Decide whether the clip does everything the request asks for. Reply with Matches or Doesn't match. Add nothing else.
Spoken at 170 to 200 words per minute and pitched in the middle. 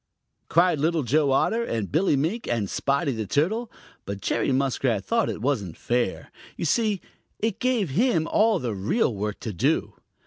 Matches